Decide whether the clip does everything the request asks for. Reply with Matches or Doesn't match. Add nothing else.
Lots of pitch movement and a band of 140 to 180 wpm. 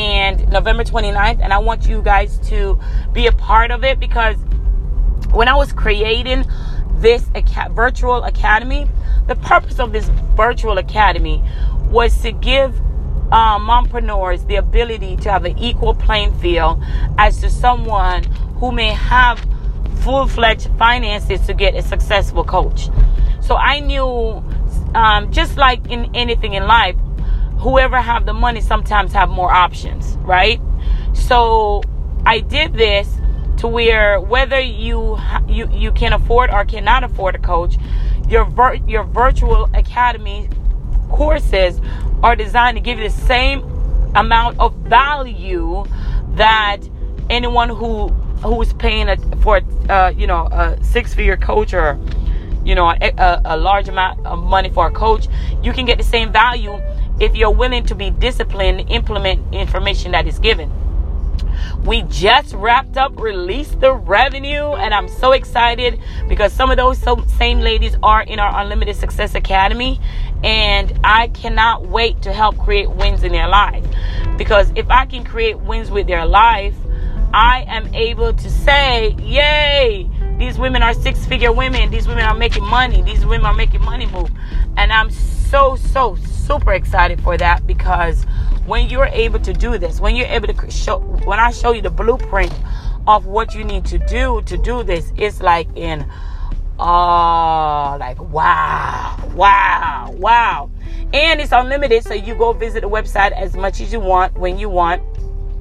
Matches